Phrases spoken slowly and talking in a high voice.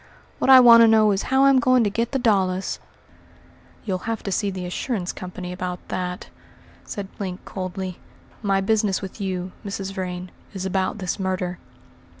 No: average, 170 wpm; high, 195 Hz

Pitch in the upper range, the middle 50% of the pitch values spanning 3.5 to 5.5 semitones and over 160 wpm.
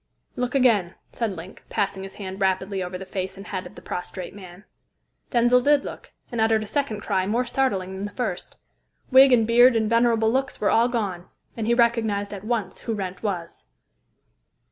Yes: high, 215 Hz; average, 3.8 semitones; average, 190 wpm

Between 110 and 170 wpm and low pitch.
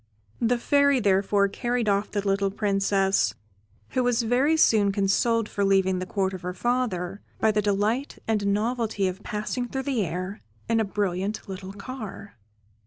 No: average, 165 wpm; high, 205 Hz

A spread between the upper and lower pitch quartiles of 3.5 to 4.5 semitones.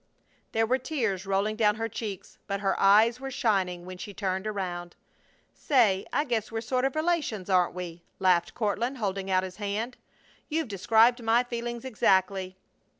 Yes: average, 4.0 semitones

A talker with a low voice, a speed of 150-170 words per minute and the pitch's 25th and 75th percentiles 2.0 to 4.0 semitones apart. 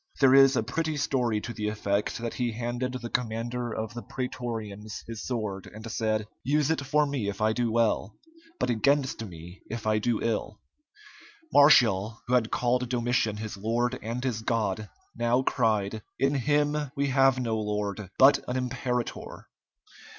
Yes: low, 120 Hz; average, 165 wpm; average, 2.9 semitones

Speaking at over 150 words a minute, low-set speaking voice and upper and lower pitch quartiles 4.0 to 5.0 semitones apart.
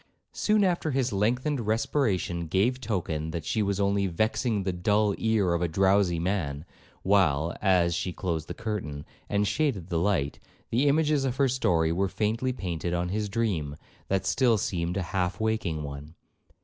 Yes: average, 170 wpm; low, 100 Hz; average, 4.6 semitones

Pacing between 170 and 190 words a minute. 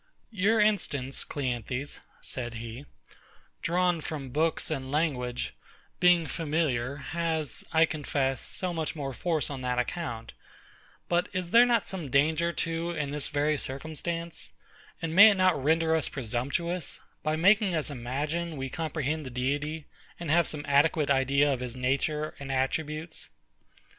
No: average, 145 wpm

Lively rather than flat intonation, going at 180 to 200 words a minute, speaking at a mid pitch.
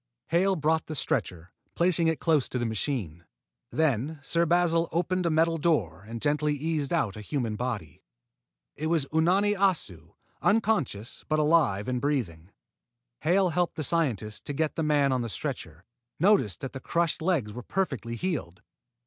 No: wide, 6.3 semitones; average, 165 wpm; medium, 150 Hz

